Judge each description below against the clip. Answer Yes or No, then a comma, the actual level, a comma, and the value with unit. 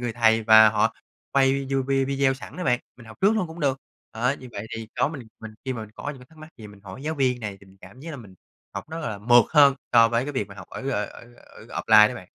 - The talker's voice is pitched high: No, low, 125 Hz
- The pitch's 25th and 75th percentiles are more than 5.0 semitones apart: No, average, 4.0 semitones